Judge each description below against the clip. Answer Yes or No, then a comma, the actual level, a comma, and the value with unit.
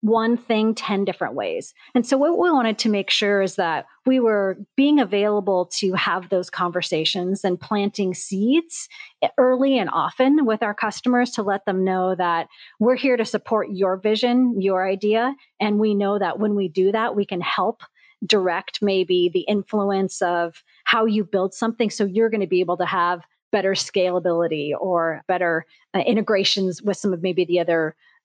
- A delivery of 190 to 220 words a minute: No, average, 180 wpm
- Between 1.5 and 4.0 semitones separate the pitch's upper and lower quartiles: Yes, average, 3.5 semitones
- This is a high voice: Yes, high, 200 Hz